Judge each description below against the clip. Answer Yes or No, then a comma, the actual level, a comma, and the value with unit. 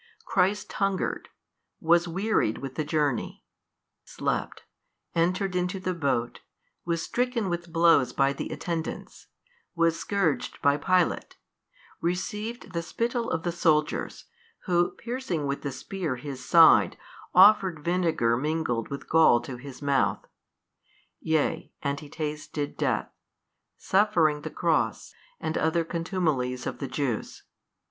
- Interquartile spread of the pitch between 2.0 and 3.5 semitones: No, average, 4.3 semitones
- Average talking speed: No, slow, 125 wpm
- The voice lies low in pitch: No, medium, 165 Hz